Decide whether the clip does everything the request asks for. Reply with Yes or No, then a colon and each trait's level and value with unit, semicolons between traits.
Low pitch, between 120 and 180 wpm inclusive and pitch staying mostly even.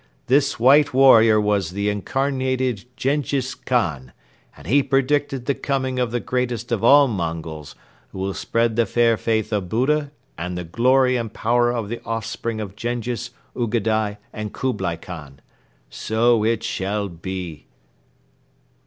No: low, 115 Hz; average, 145 wpm; average, 4.1 semitones